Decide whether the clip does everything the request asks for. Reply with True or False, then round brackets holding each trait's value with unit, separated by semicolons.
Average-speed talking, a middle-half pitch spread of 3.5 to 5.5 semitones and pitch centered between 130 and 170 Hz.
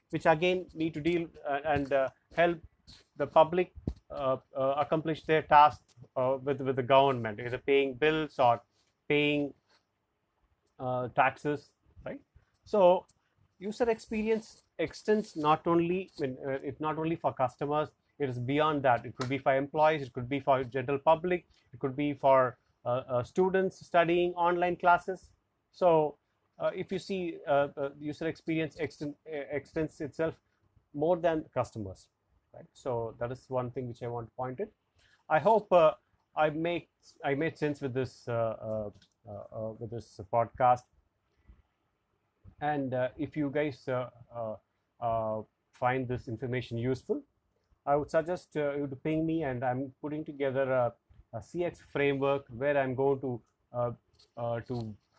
True (155 wpm; 4.7 semitones; 140 Hz)